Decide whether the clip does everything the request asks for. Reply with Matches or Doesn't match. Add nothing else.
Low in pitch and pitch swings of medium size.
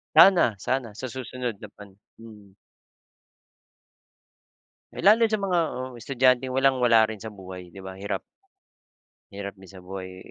Matches